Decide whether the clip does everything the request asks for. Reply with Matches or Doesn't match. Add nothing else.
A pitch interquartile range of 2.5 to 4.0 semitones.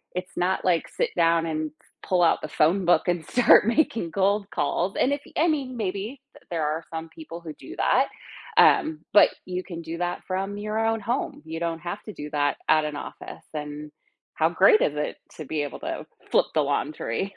Doesn't match